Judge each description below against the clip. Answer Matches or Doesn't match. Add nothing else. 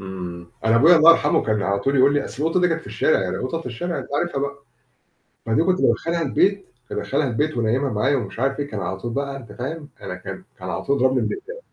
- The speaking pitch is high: Doesn't match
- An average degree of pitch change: Doesn't match